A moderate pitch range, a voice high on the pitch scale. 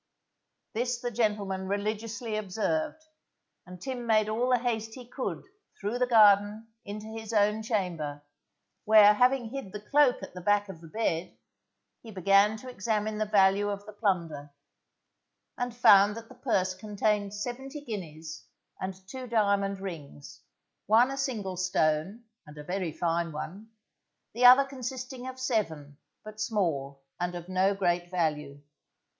Yes: average, 4.0 semitones; high, 210 Hz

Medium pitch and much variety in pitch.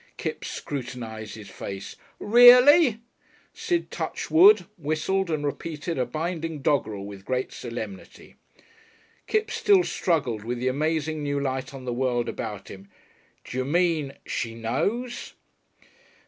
Yes: medium, 145 Hz; wide, 6.7 semitones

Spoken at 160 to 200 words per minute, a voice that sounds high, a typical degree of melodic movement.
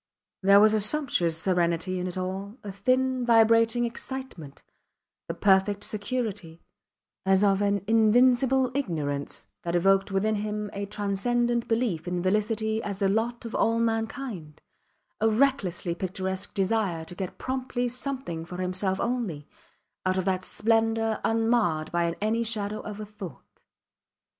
No: average, 140 wpm; high, 205 Hz; average, 3.6 semitones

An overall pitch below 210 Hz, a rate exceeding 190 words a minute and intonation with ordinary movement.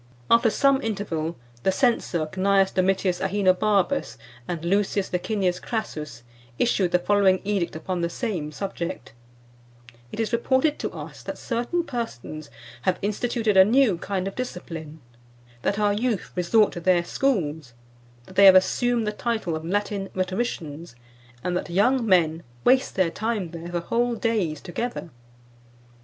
No: high, 190 Hz; average, 150 wpm; average, 4.5 semitones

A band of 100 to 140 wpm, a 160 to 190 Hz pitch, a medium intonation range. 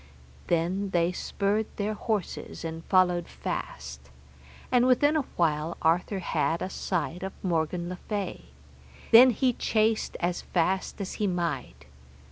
Yes: slow, 135 wpm; medium, 185 Hz; average, 3.9 semitones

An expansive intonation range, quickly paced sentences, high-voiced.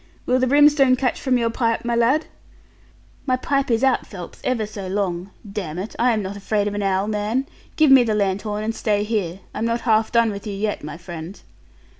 No: average, 3.7 semitones; fast, 215 wpm; high, 215 Hz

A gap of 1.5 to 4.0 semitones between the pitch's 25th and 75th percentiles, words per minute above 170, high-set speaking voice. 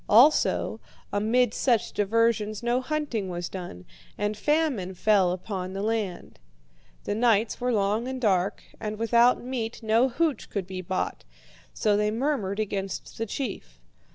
No: average, 3.6 semitones; average, 145 wpm; high, 215 Hz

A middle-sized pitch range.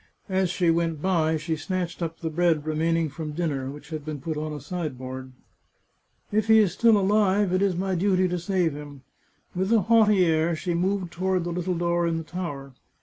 Yes: average, 3.1 semitones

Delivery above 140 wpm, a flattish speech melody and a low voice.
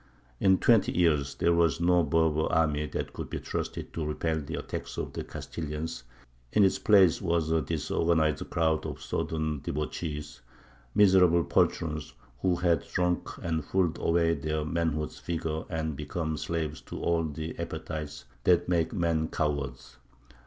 Yes: average, 150 wpm; narrow, 1.9 semitones; very low, 80 Hz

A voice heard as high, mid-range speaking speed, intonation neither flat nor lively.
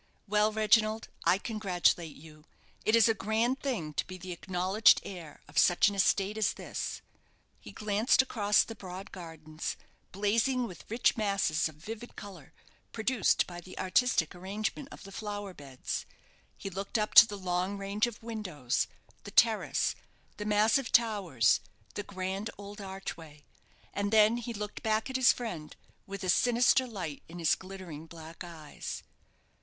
Yes: high, 200 Hz; average, 160 wpm; average, 3.6 semitones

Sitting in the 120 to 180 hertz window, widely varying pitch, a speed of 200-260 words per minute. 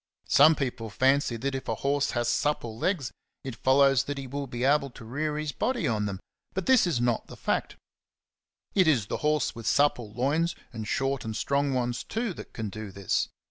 No: low, 135 Hz; average, 3.9 semitones; fast, 205 wpm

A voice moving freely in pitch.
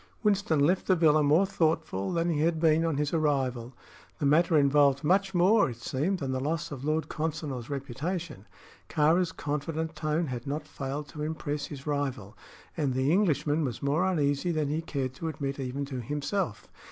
No: average, 2.9 semitones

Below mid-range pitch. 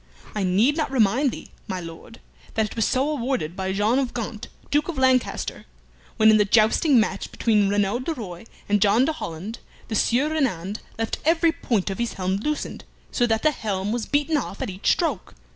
No: high, 225 Hz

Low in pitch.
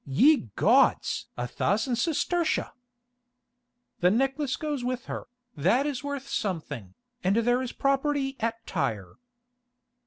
No: high, 245 Hz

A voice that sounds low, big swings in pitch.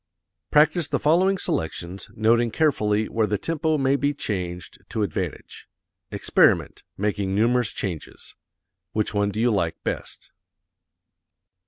Yes: low, 110 Hz; wide, 6.0 semitones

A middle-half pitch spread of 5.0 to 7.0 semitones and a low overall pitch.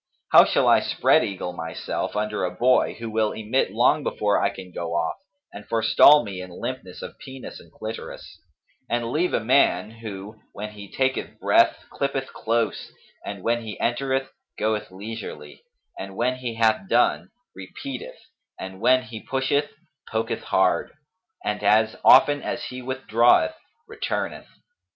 No: average, 3.7 semitones; low, 115 Hz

